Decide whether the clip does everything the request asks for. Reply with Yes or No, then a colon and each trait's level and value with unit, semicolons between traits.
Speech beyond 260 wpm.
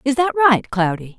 No: fast, 205 wpm